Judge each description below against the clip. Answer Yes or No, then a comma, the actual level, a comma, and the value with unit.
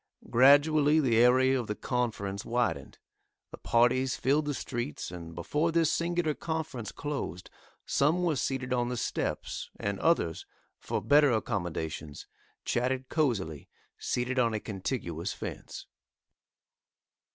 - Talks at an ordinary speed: No, slow, 125 wpm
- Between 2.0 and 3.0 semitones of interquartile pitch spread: No, wide, 5.6 semitones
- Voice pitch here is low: Yes, low, 125 Hz